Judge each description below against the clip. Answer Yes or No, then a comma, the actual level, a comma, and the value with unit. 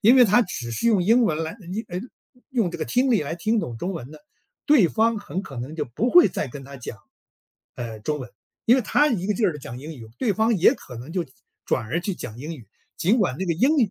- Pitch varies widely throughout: Yes, wide, 8.3 semitones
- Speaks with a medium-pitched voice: Yes, medium, 180 Hz